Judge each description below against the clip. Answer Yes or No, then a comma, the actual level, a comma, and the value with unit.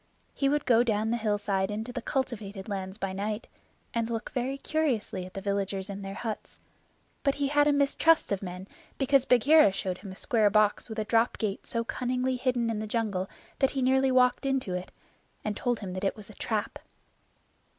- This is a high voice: Yes, high, 225 Hz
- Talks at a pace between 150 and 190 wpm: No, average, 200 wpm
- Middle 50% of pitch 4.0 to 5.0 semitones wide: Yes, average, 4.3 semitones